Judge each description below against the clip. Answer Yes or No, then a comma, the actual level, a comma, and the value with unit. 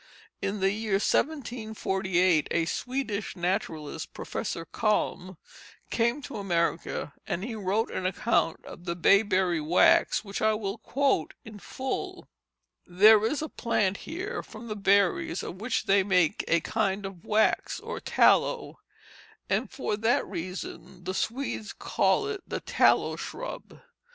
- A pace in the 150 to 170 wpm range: No, average, 140 wpm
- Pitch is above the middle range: Yes, high, 200 Hz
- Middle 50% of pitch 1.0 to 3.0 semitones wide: No, average, 3.6 semitones